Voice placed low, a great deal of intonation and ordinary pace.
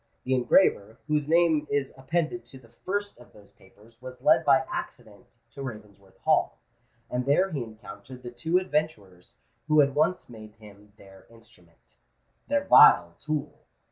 Yes: low, 125 Hz; wide, 6.3 semitones; average, 150 wpm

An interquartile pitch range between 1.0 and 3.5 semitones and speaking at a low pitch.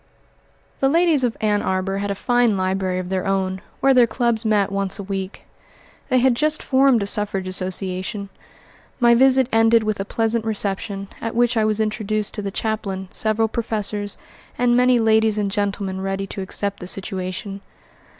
No: average, 3.1 semitones; high, 210 Hz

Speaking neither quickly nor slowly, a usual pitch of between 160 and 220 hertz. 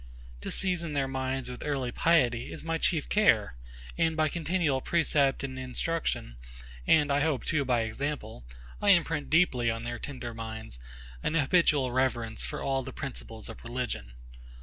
No: average, 160 wpm; low, 135 Hz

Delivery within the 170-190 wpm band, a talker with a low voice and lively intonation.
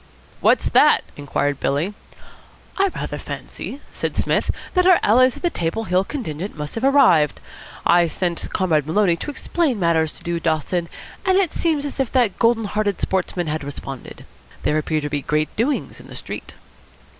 No: average, 175 wpm; medium, 185 Hz; wide, 8.5 semitones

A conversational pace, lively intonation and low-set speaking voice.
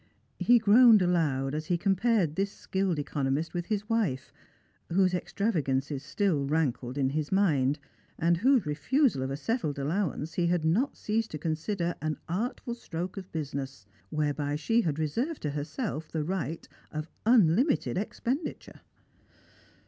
No: average, 150 wpm; wide, 5.7 semitones; medium, 170 Hz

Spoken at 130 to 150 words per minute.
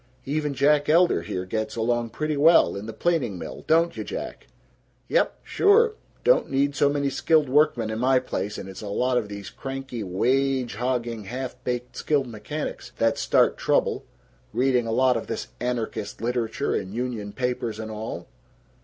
No: average, 170 wpm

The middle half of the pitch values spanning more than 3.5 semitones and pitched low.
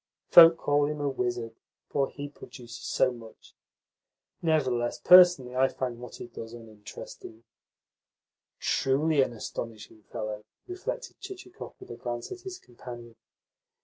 Yes: average, 4.3 semitones; low, 125 Hz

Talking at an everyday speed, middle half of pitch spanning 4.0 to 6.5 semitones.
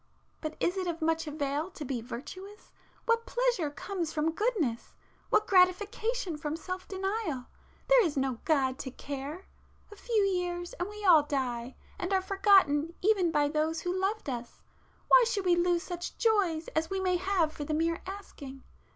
Yes: average, 170 wpm; average, 4.8 semitones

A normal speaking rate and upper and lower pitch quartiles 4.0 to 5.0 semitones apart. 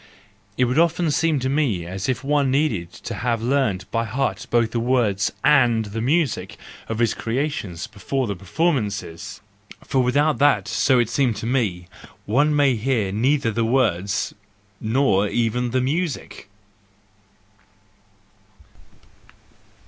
No: slow, 130 wpm; average, 4.7 semitones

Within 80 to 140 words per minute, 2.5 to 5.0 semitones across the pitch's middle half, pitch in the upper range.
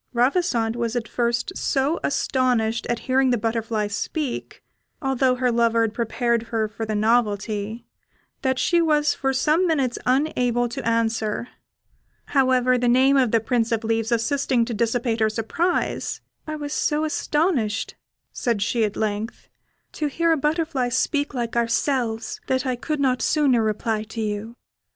No: average, 155 wpm; average, 3.1 semitones; high, 240 Hz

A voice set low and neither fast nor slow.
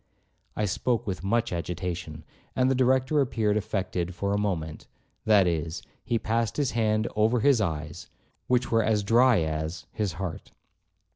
Yes: low, 105 Hz; average, 150 wpm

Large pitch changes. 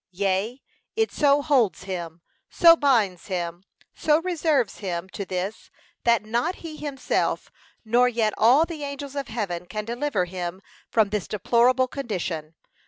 Yes: wide, 7.0 semitones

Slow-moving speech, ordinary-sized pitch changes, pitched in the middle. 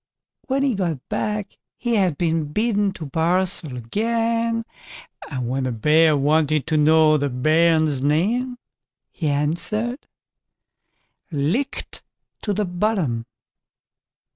No: slow, 115 wpm; wide, 6.3 semitones; medium, 165 Hz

